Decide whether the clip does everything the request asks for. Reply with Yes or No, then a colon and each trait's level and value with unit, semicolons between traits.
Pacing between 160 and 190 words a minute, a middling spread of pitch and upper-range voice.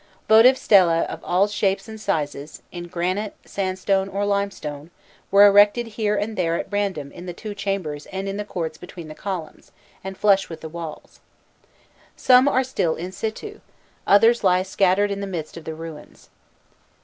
Yes: average, 175 wpm; average, 3.4 semitones; high, 195 Hz